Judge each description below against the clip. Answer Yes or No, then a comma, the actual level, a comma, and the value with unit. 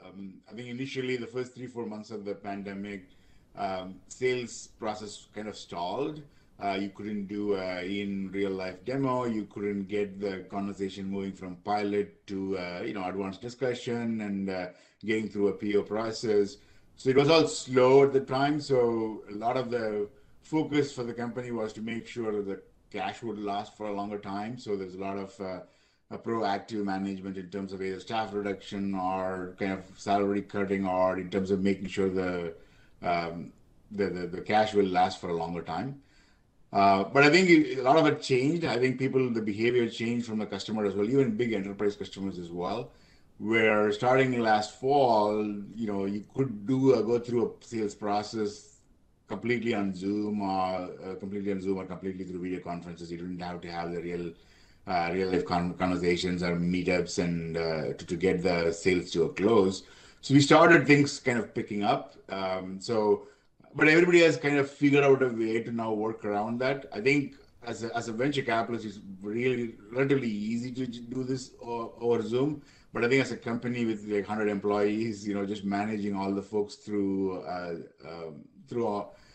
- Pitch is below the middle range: Yes, low, 105 Hz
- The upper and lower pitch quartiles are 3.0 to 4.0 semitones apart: Yes, average, 3.7 semitones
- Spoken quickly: No, average, 195 wpm